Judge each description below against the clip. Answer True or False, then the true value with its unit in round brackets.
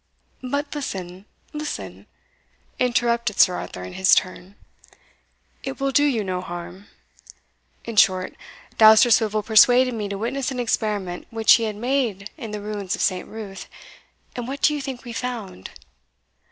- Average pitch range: True (4.4 semitones)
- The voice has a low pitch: False (220 Hz)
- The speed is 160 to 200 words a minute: False (150 wpm)